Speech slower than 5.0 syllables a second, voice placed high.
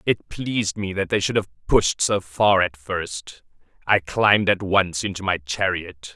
No: 4.2 syllables/s; very low, 90 Hz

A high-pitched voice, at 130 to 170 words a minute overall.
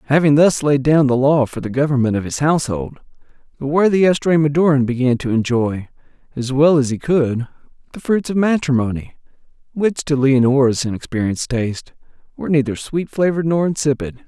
No: medium, 140 Hz; average, 160 wpm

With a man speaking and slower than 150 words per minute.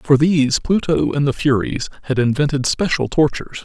No: male; average, 165 wpm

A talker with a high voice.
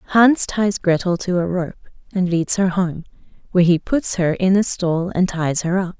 No: medium, 180 Hz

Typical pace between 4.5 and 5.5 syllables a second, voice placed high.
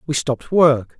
No: 4.7 syllables/s; medium, 145 Hz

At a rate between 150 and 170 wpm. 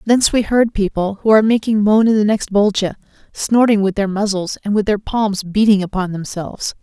No: average, 200 wpm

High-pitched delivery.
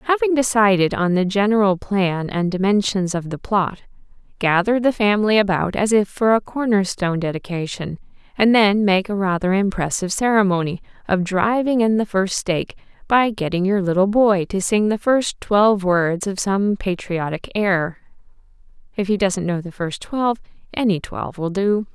Yes: high, 200 Hz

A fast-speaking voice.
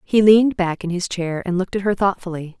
Yes: fast, 255 wpm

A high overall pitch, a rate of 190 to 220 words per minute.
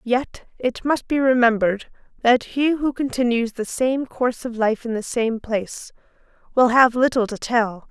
No: high, 240 Hz; average, 175 wpm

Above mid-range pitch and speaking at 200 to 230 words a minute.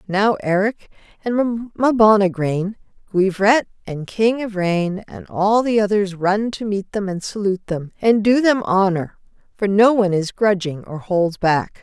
No: high, 200 Hz; average, 155 wpm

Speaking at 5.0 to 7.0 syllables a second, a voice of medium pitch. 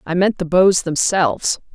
No: 4.6 syllables/s; medium, 180 Hz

